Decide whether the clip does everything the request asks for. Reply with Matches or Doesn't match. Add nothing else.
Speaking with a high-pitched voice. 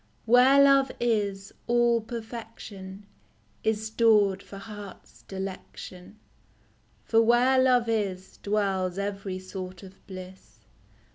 Matches